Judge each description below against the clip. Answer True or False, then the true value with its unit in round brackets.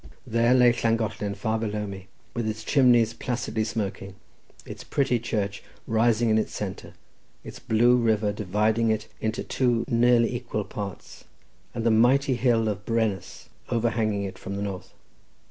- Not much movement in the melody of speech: True (2.1 semitones)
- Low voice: True (110 Hz)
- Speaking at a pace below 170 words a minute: True (150 wpm)